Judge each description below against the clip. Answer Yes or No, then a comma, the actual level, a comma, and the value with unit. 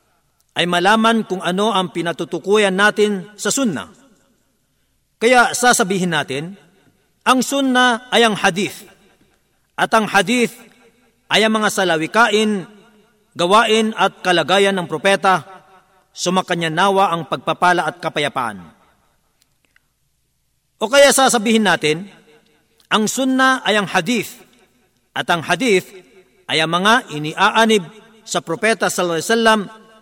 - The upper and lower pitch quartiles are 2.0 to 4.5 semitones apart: Yes, average, 4.0 semitones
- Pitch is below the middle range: No, high, 195 Hz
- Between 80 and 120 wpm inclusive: Yes, slow, 110 wpm